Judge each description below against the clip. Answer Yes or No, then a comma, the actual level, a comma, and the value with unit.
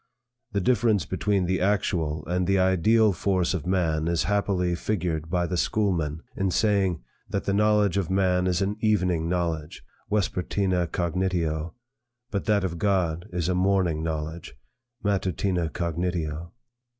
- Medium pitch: No, very low, 90 Hz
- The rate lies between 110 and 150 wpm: Yes, average, 140 wpm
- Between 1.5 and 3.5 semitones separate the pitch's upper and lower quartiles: Yes, average, 2.8 semitones